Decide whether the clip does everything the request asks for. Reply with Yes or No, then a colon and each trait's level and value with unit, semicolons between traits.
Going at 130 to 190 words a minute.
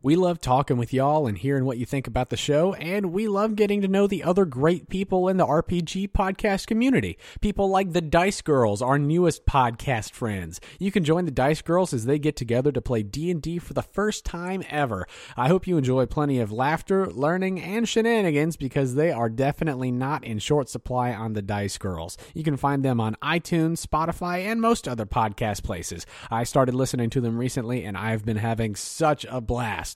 No: fast, 205 wpm